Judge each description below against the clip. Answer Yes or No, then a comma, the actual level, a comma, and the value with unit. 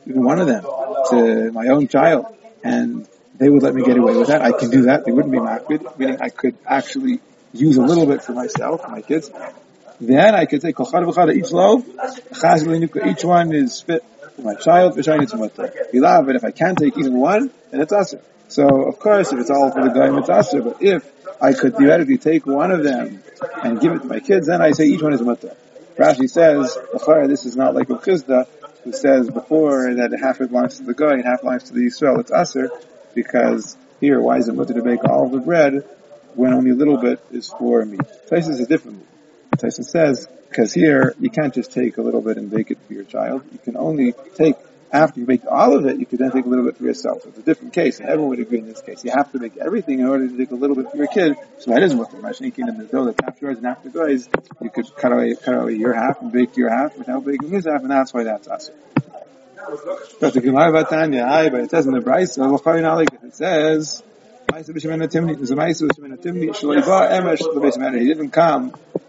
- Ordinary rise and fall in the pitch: Yes, average, 4.2 semitones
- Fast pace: Yes, fast, 225 wpm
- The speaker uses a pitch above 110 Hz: Yes, medium, 140 Hz